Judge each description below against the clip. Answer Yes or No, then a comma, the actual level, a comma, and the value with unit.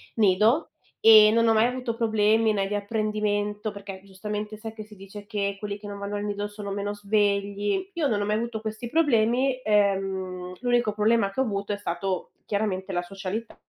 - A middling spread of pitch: No, narrow, 1.7 semitones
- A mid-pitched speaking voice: No, high, 210 Hz